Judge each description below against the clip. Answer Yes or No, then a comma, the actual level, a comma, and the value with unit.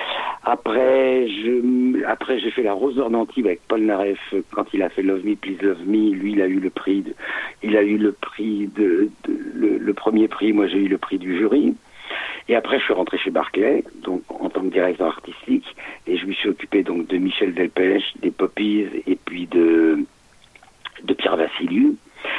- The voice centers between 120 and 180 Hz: No, low, 110 Hz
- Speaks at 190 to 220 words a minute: Yes, average, 200 wpm